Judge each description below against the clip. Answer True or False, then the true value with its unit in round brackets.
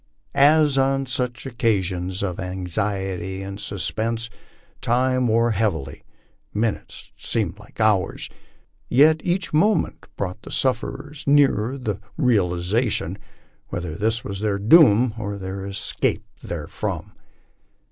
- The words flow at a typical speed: False (110 wpm)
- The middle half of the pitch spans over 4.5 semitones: True (5.1 semitones)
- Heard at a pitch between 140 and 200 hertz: False (110 Hz)